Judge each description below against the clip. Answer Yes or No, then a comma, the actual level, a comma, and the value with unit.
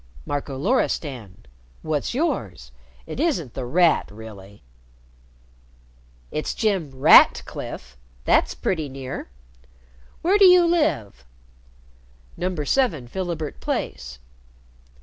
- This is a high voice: No, medium, 145 Hz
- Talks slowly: Yes, slow, 90 wpm